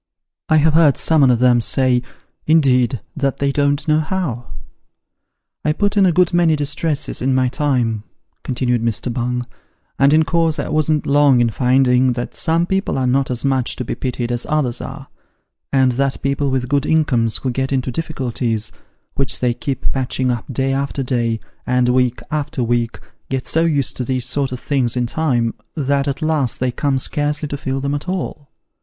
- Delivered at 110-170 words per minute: No, average, 190 wpm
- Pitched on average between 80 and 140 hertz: Yes, low, 135 Hz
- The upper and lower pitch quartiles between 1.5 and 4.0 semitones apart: Yes, average, 3.0 semitones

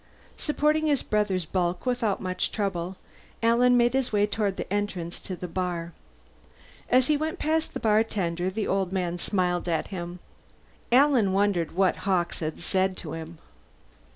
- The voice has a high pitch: Yes, high, 195 Hz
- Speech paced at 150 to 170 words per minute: Yes, average, 155 wpm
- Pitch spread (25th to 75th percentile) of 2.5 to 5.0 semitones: Yes, average, 4.7 semitones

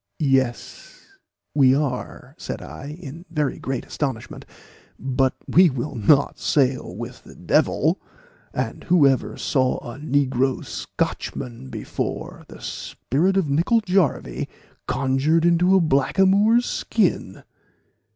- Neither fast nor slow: No, slow, 115 wpm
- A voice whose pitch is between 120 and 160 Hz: Yes, medium, 140 Hz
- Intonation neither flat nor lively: Yes, average, 4.7 semitones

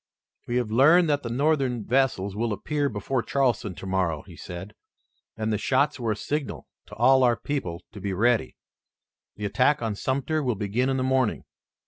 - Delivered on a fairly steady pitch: No, average, 4.6 semitones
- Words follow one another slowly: No, average, 180 wpm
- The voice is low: Yes, low, 120 Hz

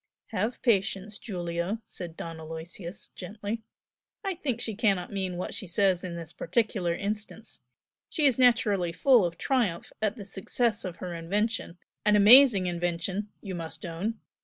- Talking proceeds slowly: No, average, 155 wpm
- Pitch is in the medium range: No, high, 195 Hz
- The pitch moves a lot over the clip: No, average, 4.2 semitones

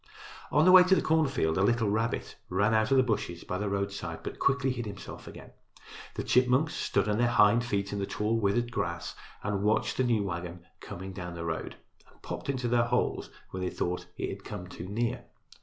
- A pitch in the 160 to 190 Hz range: No, low, 105 Hz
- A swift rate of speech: Yes, fast, 215 wpm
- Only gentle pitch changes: No, average, 4.1 semitones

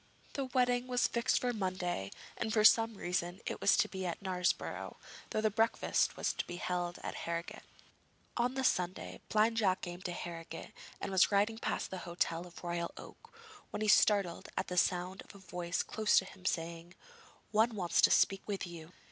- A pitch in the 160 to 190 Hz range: Yes, medium, 185 Hz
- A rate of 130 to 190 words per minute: No, average, 200 wpm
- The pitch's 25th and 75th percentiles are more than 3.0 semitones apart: Yes, average, 3.7 semitones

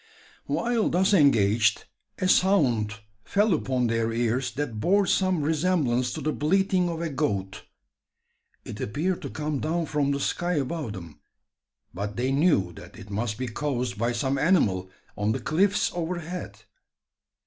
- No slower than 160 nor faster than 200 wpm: No, average, 150 wpm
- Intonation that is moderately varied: No, wide, 7.3 semitones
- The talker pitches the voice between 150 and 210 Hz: No, medium, 140 Hz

